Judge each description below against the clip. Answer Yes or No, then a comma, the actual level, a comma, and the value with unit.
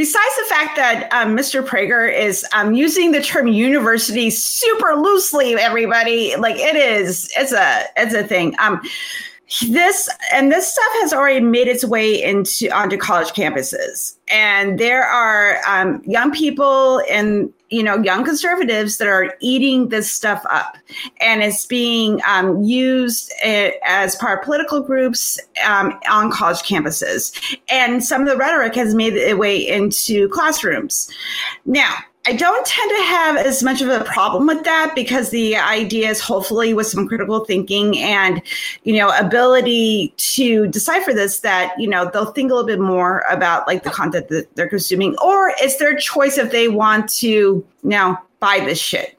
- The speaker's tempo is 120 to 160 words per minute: No, average, 170 wpm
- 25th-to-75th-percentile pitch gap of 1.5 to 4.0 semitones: No, average, 5.2 semitones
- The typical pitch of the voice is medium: No, high, 235 Hz